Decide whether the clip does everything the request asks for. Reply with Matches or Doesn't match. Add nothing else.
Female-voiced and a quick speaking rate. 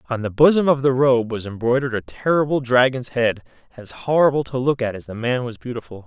Doesn't match